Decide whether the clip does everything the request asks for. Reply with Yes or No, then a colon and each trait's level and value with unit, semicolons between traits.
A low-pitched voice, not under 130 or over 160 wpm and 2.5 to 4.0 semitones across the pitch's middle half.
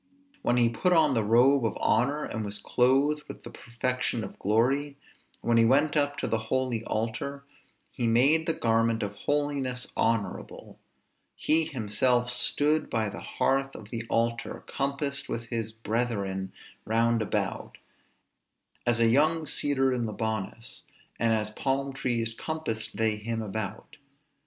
Yes: low, 120 Hz; average, 145 wpm; average, 3.7 semitones